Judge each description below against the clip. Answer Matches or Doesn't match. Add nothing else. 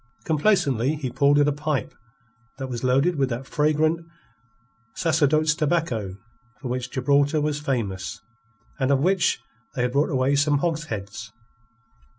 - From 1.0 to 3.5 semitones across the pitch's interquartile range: Matches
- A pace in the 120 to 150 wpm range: Matches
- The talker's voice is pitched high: Doesn't match